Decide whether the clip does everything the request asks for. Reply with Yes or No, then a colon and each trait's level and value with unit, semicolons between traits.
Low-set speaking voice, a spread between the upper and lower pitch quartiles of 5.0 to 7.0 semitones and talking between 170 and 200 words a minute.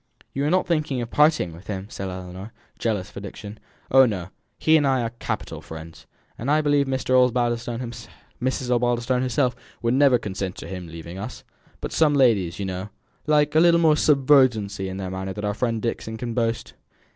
Yes: low, 115 Hz; wide, 5.5 semitones; average, 180 wpm